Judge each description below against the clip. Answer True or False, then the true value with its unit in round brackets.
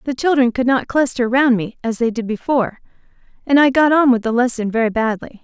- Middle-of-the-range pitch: False (245 Hz)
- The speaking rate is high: True (220 wpm)